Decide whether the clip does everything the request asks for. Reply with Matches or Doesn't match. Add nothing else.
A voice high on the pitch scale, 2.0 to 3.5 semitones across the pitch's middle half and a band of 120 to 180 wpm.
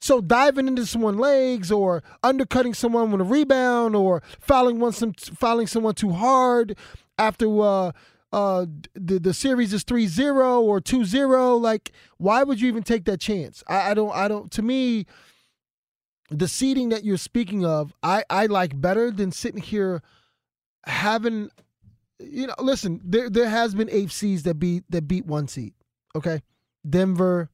Doesn't match